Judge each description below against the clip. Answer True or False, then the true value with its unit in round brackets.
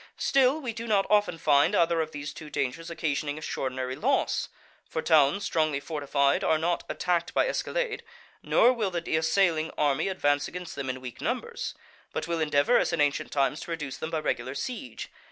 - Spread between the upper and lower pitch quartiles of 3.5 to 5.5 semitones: True (4.5 semitones)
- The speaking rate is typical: True (185 wpm)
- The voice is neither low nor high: True (160 Hz)